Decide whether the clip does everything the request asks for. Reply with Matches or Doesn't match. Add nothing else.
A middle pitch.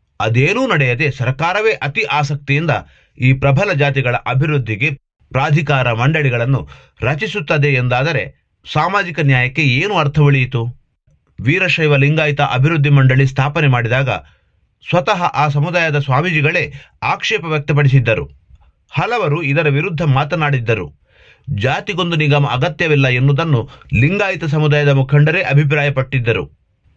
Matches